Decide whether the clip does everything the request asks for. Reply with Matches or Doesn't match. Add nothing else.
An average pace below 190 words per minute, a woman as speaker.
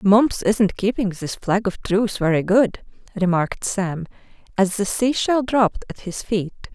Matches